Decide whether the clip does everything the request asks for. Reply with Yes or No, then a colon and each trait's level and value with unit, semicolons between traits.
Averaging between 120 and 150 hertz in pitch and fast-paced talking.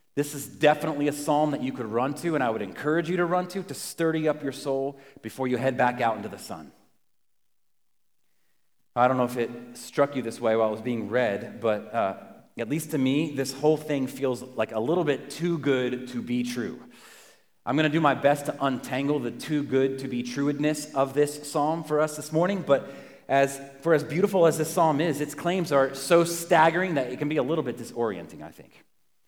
Yes: medium, 140 Hz; fast, 225 wpm